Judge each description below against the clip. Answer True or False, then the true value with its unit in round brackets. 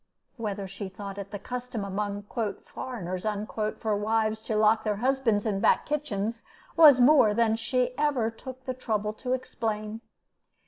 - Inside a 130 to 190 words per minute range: True (150 wpm)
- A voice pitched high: True (220 Hz)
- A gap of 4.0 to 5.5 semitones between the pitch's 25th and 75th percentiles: False (3.4 semitones)